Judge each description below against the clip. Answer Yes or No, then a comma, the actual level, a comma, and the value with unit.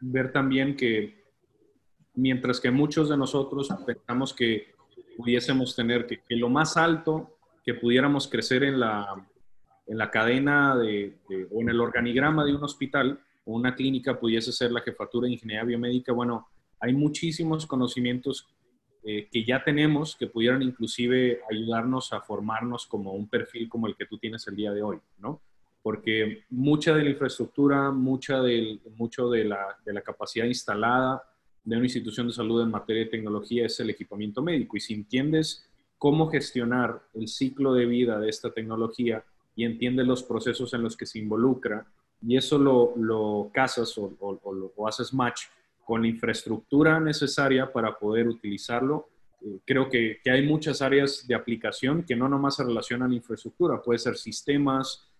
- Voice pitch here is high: No, low, 120 Hz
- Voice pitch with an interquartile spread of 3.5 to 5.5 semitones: No, average, 2.9 semitones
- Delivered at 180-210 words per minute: No, average, 165 wpm